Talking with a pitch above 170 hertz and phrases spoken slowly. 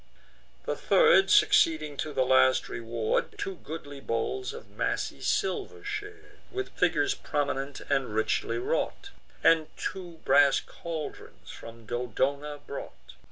No: medium, 150 Hz; slow, 120 wpm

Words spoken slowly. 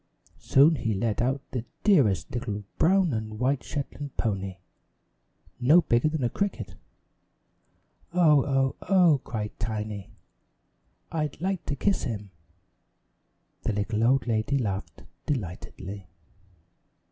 Yes: slow, 115 wpm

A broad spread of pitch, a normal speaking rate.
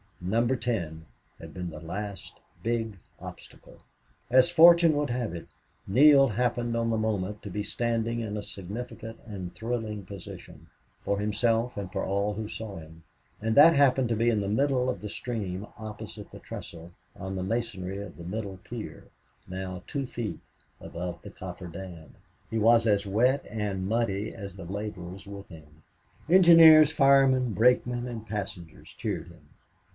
No: average, 4.0 semitones; average, 160 wpm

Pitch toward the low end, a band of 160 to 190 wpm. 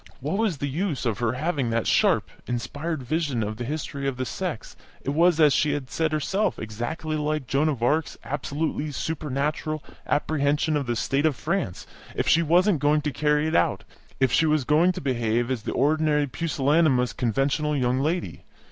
No: medium, 145 Hz; average, 185 wpm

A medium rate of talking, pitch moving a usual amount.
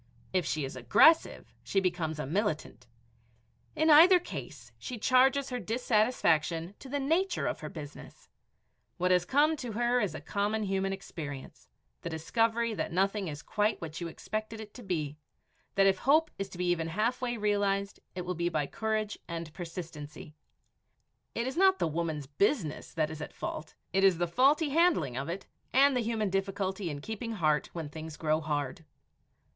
No: average, 175 wpm; wide, 6.4 semitones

